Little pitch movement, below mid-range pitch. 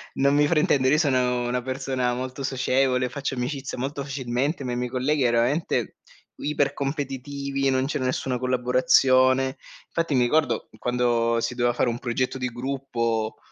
Yes: narrow, 2.0 semitones; low, 130 Hz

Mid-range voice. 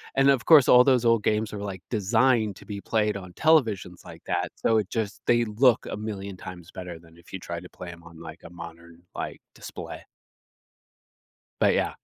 No: low, 100 Hz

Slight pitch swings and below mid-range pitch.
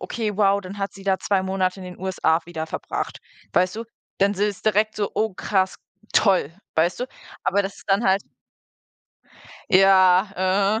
No: narrow, 1.6 semitones; high, 195 Hz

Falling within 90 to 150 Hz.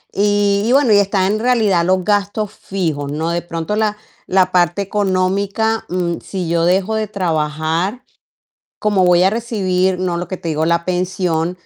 No: medium, 185 Hz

